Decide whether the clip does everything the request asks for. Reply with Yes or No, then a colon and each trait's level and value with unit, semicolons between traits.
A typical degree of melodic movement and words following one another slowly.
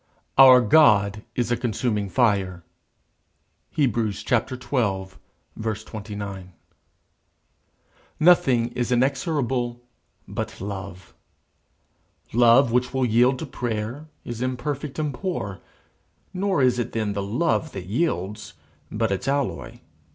Yes: average, 4.3 semitones; slow, 105 wpm